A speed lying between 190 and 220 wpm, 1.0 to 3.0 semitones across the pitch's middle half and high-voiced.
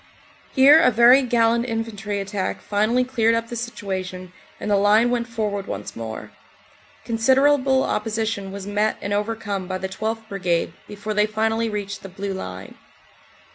No: average, 155 wpm; narrow, 2.5 semitones; high, 215 Hz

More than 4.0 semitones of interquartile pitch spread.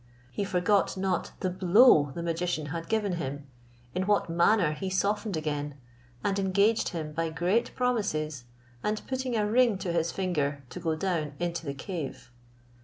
Yes: average, 4.5 semitones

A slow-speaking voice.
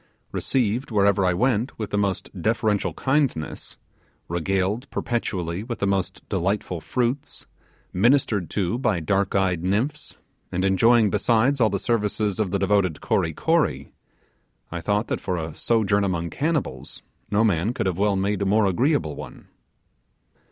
No: average, 150 wpm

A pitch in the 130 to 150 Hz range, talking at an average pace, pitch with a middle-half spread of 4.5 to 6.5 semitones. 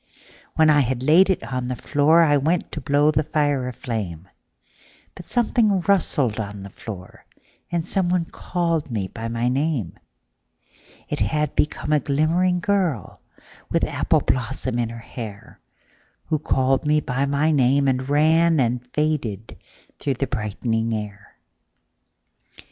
No: medium, 140 Hz; slow, 125 wpm; average, 5.1 semitones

